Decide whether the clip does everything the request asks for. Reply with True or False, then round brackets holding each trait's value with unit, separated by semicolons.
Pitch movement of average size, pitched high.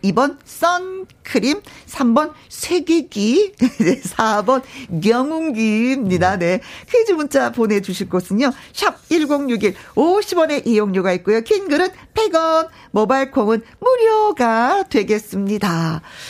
False (7.6 semitones; 260 Hz)